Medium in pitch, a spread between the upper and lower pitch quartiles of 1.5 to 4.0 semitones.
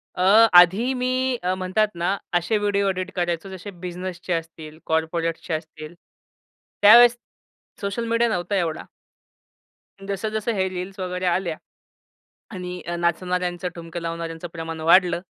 Yes: medium, 180 Hz; average, 2.8 semitones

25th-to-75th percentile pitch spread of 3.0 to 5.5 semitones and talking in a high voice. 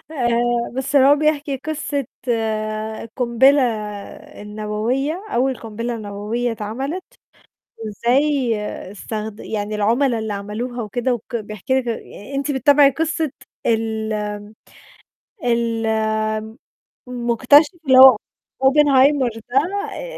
Yes: average, 3.9 semitones; high, 245 Hz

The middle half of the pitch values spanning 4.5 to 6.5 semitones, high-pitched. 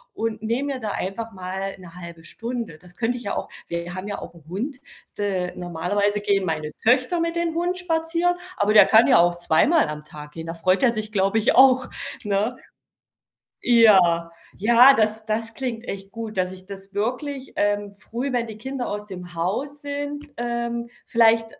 Yes: average, 4.9 semitones; high, 215 Hz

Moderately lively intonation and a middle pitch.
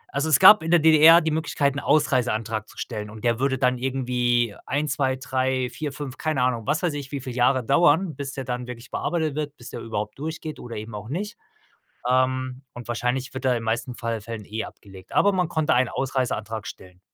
No: average, 3.8 semitones; low, 130 Hz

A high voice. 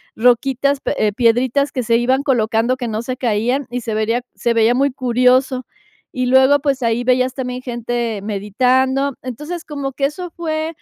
Yes: very high, 255 Hz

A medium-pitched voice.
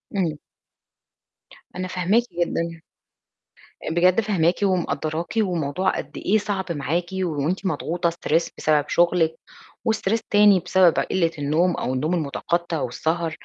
Yes: medium, 175 Hz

